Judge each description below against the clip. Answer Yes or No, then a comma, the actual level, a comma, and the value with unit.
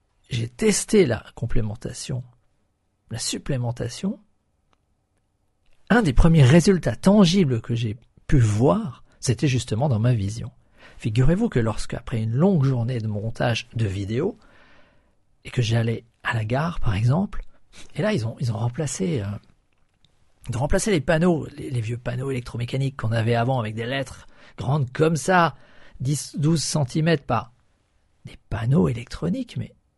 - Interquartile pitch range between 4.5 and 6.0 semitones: Yes, average, 4.9 semitones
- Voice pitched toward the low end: Yes, low, 125 Hz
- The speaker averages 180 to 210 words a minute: No, slow, 145 wpm